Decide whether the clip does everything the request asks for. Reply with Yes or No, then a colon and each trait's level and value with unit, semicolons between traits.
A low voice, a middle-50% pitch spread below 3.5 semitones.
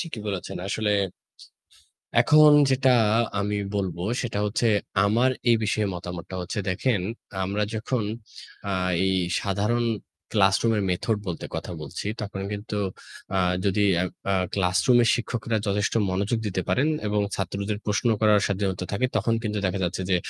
Yes: low, 105 Hz; average, 2.9 semitones